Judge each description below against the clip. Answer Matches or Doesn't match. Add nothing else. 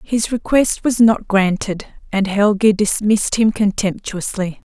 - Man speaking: Doesn't match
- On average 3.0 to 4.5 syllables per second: Matches